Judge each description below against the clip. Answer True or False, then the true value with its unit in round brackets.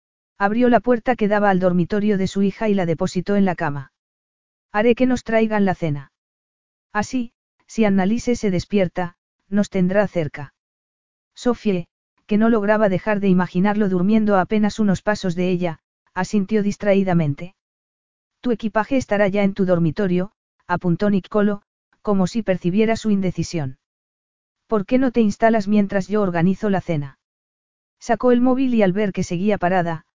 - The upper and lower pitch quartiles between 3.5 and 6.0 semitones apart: False (3.1 semitones)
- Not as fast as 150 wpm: False (155 wpm)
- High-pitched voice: True (200 Hz)